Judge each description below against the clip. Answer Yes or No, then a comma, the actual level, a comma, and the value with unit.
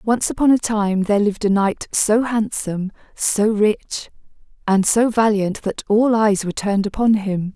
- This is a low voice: No, high, 210 Hz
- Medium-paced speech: Yes, average, 175 wpm